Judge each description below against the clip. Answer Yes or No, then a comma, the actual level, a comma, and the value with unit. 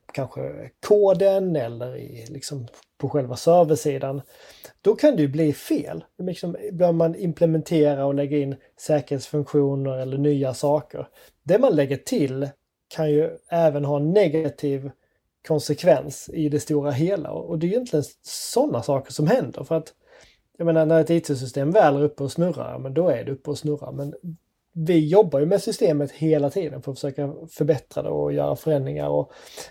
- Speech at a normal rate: Yes, average, 170 wpm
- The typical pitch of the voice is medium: Yes, medium, 150 Hz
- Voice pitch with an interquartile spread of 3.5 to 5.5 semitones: No, average, 2.9 semitones